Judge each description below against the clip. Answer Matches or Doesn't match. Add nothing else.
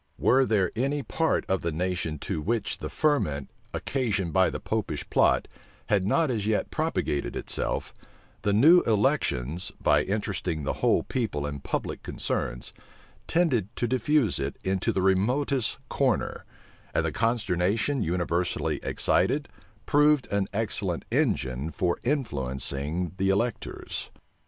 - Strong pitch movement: Matches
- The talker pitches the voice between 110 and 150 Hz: Doesn't match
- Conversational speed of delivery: Doesn't match